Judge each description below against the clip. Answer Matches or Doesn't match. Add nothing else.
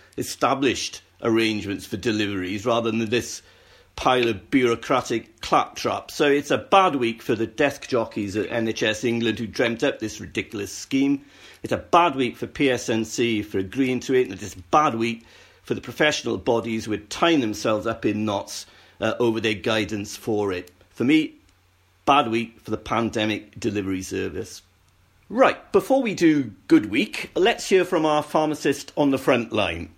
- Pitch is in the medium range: Doesn't match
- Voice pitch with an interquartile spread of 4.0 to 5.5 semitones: Matches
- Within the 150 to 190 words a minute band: Matches